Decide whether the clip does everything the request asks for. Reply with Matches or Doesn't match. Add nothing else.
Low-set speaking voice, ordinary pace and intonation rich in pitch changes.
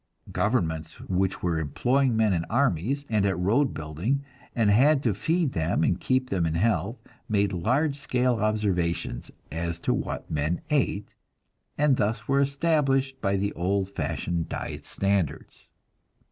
Matches